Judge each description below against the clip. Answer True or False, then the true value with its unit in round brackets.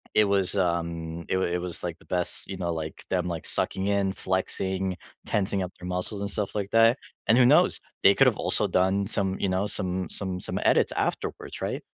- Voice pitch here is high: False (95 Hz)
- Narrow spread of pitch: True (1.9 semitones)